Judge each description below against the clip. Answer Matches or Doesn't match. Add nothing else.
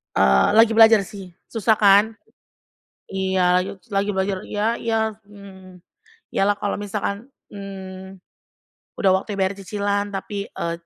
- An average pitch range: Doesn't match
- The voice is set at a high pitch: Matches